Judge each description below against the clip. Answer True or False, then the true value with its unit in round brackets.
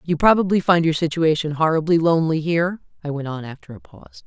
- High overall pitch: False (155 Hz)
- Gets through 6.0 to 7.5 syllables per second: True (6.4 syllables/s)